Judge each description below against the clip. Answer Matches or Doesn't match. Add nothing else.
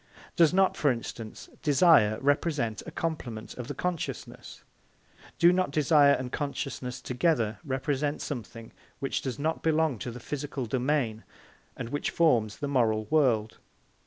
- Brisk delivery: Doesn't match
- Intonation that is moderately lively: Matches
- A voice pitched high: Doesn't match